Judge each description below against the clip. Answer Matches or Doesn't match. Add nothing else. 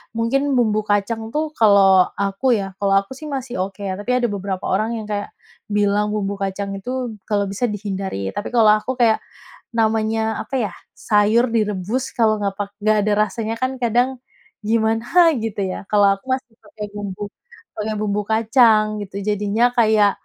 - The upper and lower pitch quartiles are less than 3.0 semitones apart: Matches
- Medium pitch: Doesn't match